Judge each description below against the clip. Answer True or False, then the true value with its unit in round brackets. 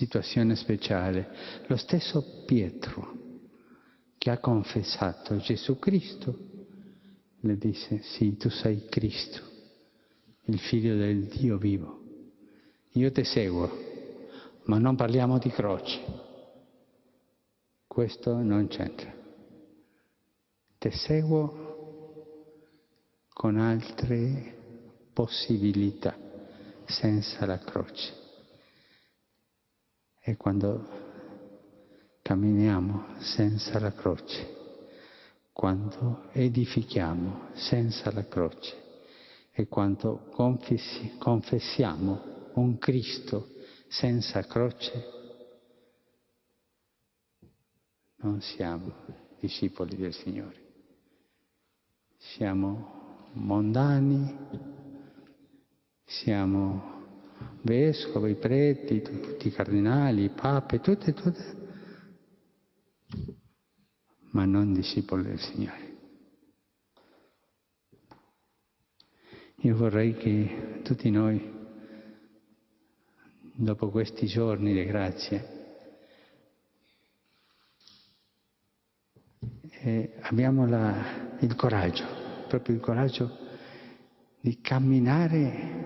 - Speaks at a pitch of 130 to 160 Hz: False (115 Hz)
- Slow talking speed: True (70 wpm)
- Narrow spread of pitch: False (3.7 semitones)